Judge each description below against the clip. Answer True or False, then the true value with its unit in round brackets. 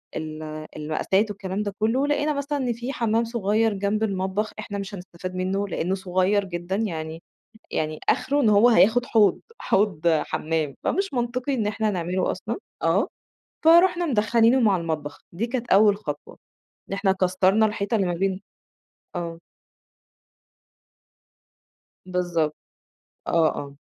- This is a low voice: False (200 Hz)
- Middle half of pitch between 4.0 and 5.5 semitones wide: True (4.3 semitones)